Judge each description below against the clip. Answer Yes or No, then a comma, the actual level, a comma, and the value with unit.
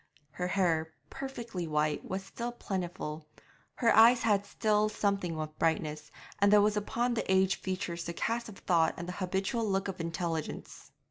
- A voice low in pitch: No, high, 190 Hz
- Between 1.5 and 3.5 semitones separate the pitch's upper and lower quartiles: No, average, 4.1 semitones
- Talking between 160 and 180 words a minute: Yes, average, 165 wpm